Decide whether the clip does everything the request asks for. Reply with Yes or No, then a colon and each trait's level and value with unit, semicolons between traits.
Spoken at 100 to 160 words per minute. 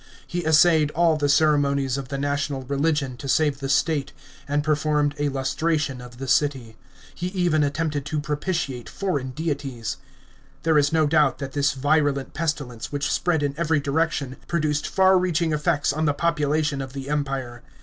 No: average, 170 wpm